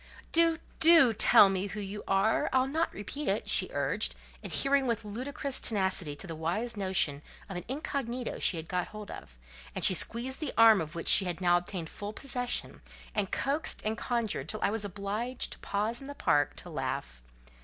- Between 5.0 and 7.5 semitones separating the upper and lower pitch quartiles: Yes, average, 5.3 semitones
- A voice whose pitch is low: No, high, 210 Hz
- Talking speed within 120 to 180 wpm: No, average, 190 wpm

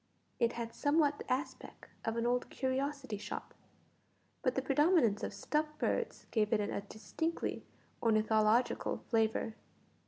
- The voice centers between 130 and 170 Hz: No, high, 245 Hz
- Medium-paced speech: No, slow, 130 wpm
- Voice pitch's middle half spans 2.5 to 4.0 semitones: No, average, 4.6 semitones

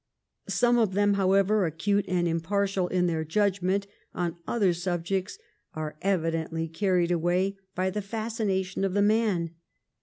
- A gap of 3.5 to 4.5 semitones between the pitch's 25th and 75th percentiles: No, average, 2.7 semitones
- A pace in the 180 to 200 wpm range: No, average, 140 wpm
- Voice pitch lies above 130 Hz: Yes, high, 190 Hz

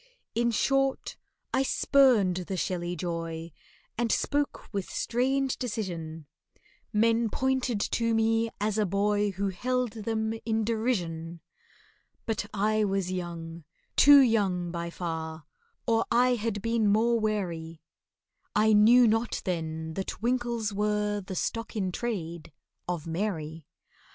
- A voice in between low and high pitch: No, high, 210 Hz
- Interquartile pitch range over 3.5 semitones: Yes, average, 4.9 semitones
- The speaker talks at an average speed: No, slow, 125 wpm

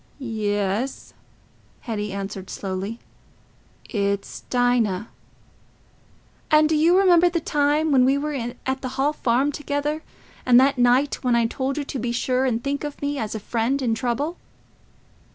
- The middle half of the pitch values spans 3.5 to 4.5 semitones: Yes, average, 4.1 semitones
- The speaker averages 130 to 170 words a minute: Yes, average, 150 wpm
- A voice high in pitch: Yes, very high, 255 Hz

